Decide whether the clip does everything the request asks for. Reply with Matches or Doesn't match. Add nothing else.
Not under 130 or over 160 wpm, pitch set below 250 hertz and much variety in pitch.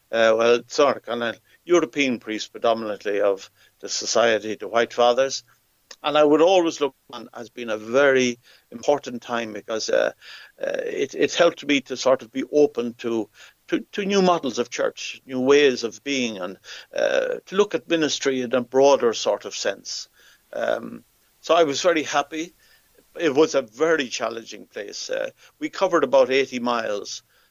Doesn't match